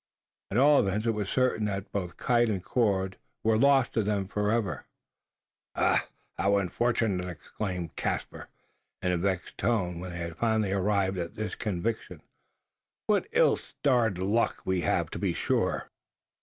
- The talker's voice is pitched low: Yes, low, 100 Hz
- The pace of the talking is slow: No, average, 160 wpm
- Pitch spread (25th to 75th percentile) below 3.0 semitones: No, average, 3.5 semitones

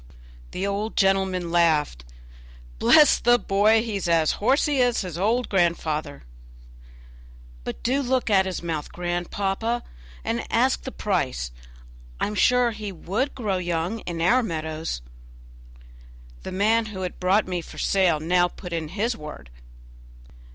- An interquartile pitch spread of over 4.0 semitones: Yes, average, 4.7 semitones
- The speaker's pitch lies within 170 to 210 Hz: Yes, high, 190 Hz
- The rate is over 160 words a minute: No, average, 145 wpm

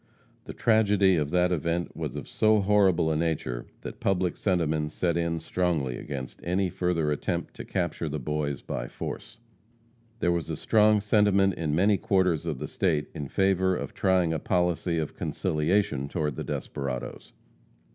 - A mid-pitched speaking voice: No, very low, 85 Hz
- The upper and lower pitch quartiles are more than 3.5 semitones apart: Yes, average, 4.0 semitones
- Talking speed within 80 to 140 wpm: No, average, 165 wpm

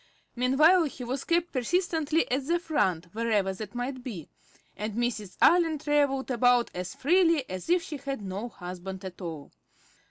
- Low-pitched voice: No, very high, 250 Hz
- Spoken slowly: No, average, 160 wpm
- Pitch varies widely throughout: Yes, wide, 7.6 semitones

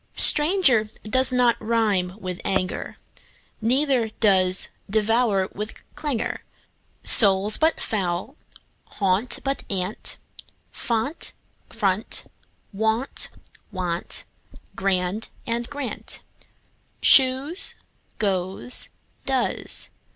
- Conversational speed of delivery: No, slow, 85 wpm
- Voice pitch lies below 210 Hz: No, high, 220 Hz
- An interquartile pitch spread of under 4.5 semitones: No, average, 5.0 semitones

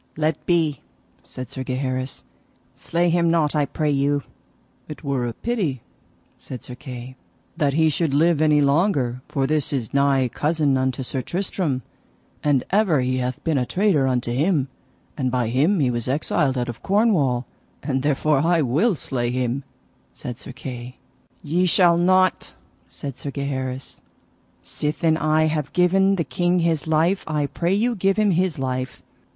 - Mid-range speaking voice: Yes, medium, 145 Hz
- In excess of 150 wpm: Yes, average, 160 wpm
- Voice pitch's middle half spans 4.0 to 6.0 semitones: Yes, average, 4.5 semitones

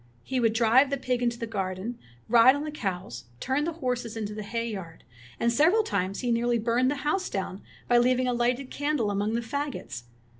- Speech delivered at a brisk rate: Yes, fast, 210 wpm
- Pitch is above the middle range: Yes, high, 240 Hz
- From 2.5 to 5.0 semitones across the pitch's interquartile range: Yes, average, 3.5 semitones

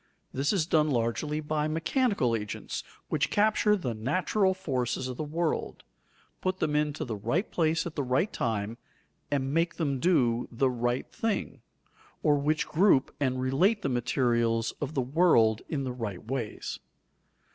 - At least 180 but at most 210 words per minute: No, average, 155 wpm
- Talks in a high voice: No, medium, 140 Hz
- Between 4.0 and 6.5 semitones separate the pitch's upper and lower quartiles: Yes, average, 5.2 semitones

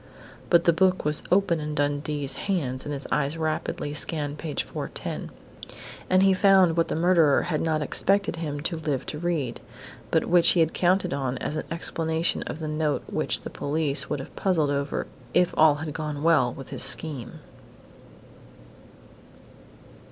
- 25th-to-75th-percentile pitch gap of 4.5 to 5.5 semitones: No, average, 2.8 semitones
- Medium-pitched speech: Yes, medium, 155 Hz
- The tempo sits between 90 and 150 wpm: No, average, 170 wpm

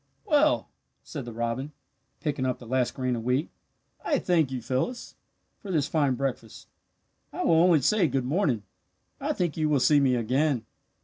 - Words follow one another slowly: No, average, 175 wpm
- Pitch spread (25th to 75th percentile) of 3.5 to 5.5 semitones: Yes, average, 4.3 semitones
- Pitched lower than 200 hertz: Yes, medium, 140 Hz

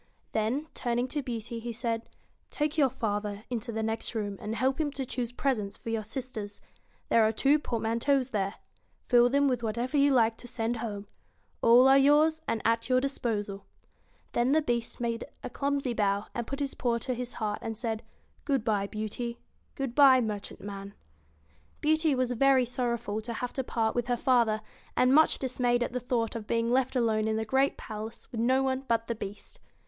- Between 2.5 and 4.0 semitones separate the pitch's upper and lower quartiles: Yes, average, 2.9 semitones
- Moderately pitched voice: No, high, 235 Hz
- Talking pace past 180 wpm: Yes, average, 195 wpm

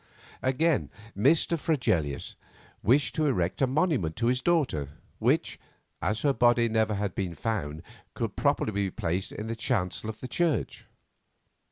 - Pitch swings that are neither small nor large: No, wide, 6.4 semitones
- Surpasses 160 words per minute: No, average, 150 wpm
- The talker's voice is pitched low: Yes, low, 110 Hz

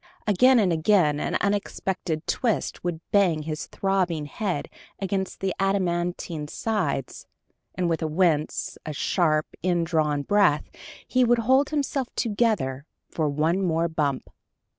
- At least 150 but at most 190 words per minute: No, slow, 135 wpm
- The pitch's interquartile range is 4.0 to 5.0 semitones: Yes, average, 4.6 semitones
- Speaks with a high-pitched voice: No, medium, 175 Hz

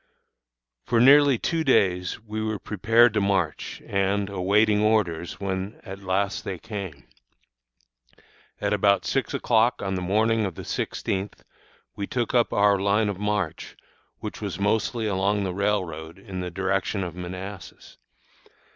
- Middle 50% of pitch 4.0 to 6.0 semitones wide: No, narrow, 2.5 semitones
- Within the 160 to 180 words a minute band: No, average, 145 wpm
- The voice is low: Yes, low, 100 Hz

